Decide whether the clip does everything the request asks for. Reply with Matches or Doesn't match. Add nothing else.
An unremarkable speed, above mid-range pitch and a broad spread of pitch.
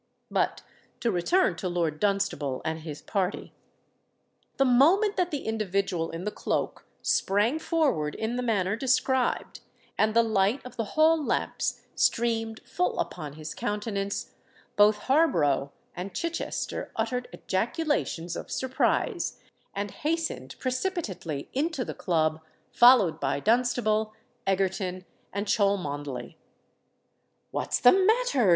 Doesn't match